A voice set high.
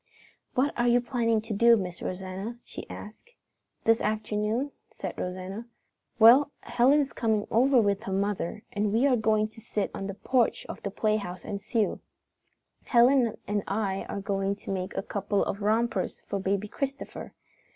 Yes: high, 215 Hz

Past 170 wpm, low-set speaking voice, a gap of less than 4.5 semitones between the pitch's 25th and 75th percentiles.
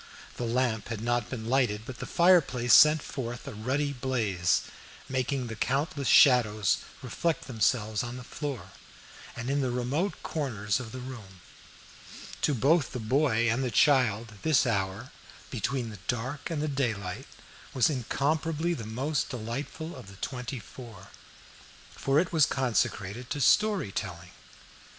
No: average, 150 wpm; low, 125 Hz; average, 4.1 semitones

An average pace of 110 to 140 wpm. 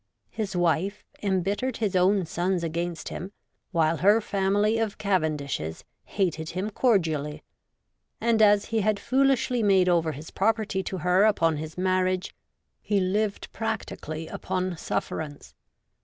Yes: slow, 135 wpm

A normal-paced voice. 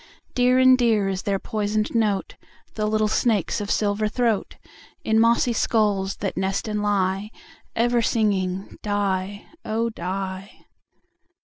No: slow, 130 wpm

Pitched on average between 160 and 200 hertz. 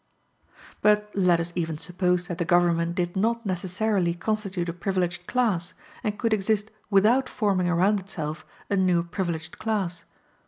Yes: medium, 185 Hz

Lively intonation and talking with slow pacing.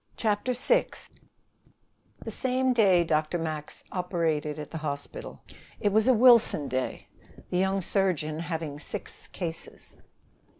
Yes: wide, 5.8 semitones; slow, 125 wpm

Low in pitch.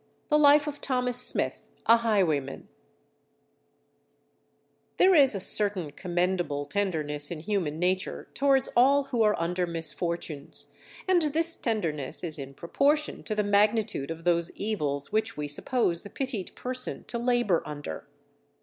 No: high, 200 Hz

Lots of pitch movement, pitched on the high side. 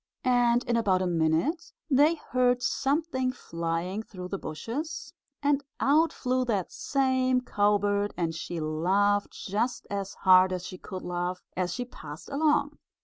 Yes: wide, 6.1 semitones; high, 210 Hz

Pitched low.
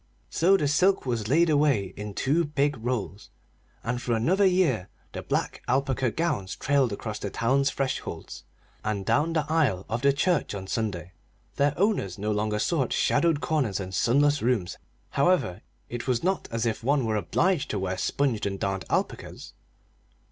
Yes: low, 125 Hz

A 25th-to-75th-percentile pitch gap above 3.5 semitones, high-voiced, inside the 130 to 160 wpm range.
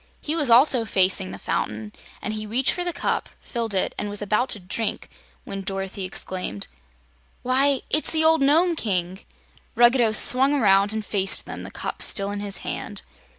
No: average, 5.2 semitones; high, 215 Hz; average, 180 wpm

